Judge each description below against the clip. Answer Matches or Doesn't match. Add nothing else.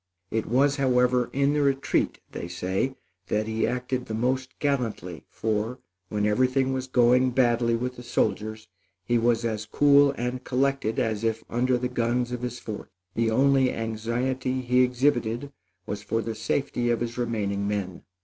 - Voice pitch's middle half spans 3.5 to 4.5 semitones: Doesn't match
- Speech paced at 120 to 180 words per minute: Matches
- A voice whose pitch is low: Matches